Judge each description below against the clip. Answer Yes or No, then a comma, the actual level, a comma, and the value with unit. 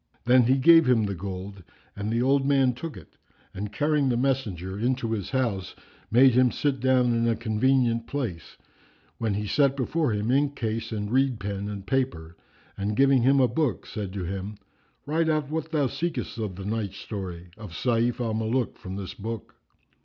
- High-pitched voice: No, low, 115 Hz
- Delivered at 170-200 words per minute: Yes, average, 190 wpm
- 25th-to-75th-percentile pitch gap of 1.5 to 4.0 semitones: No, average, 4.7 semitones